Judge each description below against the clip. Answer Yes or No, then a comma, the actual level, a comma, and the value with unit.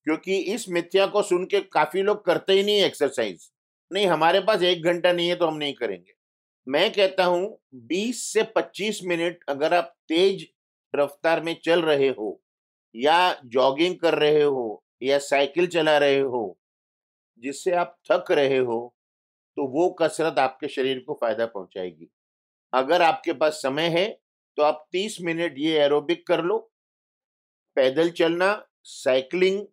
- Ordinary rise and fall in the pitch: Yes, average, 4.4 semitones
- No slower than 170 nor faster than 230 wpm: No, average, 155 wpm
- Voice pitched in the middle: Yes, medium, 165 Hz